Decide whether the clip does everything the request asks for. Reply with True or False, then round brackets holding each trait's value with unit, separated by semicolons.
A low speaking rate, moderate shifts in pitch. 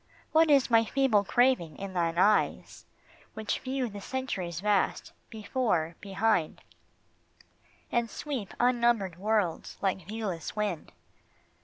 True (115 wpm; 4.4 semitones)